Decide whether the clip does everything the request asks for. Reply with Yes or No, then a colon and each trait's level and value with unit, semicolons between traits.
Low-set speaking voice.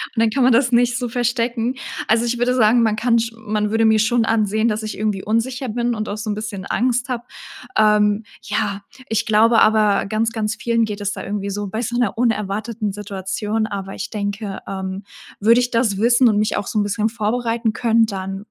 No: high, 220 Hz